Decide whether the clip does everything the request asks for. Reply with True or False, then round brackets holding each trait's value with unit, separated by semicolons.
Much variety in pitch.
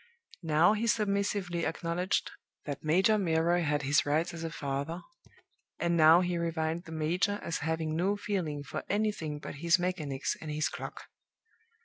False (2.9 semitones)